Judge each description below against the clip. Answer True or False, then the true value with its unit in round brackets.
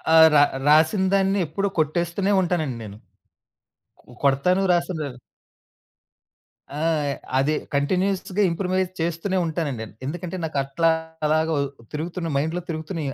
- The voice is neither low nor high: True (165 Hz)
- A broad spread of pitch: False (3.3 semitones)